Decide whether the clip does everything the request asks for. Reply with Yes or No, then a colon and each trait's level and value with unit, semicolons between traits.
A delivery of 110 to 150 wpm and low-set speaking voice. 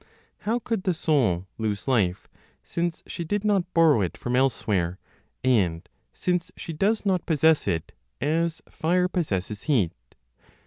No: average, 140 wpm; medium, 155 Hz